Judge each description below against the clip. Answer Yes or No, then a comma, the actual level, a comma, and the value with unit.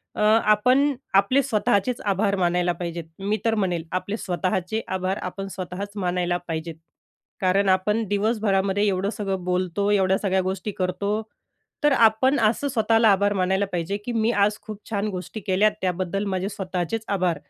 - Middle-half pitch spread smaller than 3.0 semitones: Yes, narrow, 2.5 semitones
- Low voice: No, high, 195 Hz